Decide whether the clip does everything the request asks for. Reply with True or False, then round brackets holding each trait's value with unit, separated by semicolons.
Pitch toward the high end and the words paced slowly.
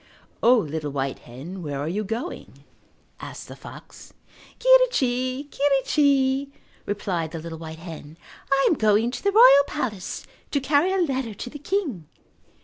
False (245 Hz; 150 wpm)